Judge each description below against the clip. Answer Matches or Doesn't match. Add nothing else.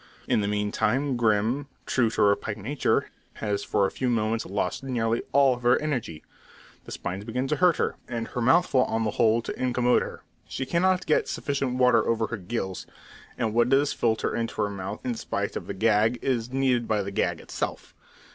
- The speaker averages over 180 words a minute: Matches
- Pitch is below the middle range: Matches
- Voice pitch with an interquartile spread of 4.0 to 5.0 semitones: Doesn't match